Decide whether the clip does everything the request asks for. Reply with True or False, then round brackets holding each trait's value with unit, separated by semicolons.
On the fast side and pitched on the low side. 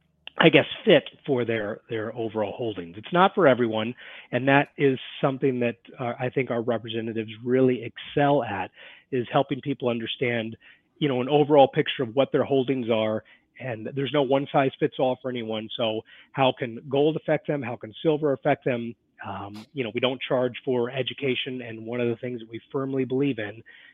False (195 wpm; 125 Hz)